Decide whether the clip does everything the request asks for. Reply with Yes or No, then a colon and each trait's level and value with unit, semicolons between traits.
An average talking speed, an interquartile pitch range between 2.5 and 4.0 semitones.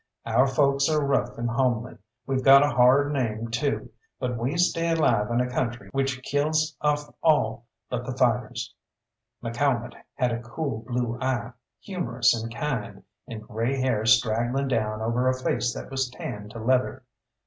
Yes: average, 165 wpm; average, 2.9 semitones